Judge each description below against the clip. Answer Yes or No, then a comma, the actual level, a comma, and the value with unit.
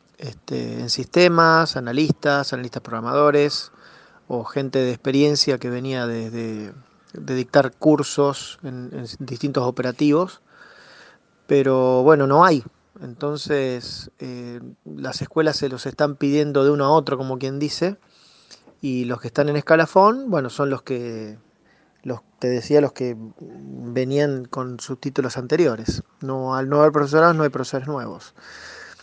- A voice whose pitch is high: No, low, 135 Hz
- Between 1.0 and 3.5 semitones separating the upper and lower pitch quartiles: Yes, average, 2.8 semitones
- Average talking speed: Yes, average, 145 wpm